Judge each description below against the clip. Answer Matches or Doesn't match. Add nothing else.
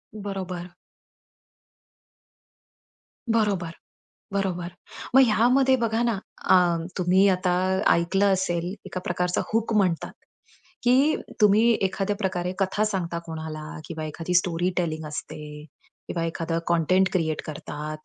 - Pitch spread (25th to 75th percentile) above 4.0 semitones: Doesn't match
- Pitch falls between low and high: Matches